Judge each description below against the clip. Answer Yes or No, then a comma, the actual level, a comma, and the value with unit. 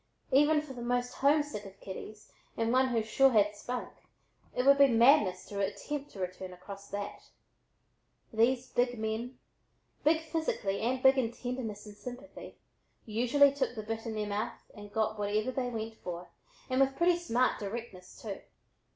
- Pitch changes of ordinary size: Yes, average, 4.0 semitones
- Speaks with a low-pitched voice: No, high, 230 Hz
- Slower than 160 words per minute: No, average, 170 wpm